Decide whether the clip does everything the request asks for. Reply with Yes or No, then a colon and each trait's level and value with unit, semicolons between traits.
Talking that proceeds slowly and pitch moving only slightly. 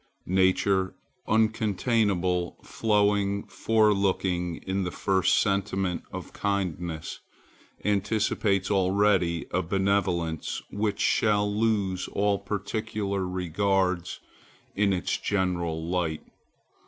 Yes: slow, 85 wpm; narrow, 2.2 semitones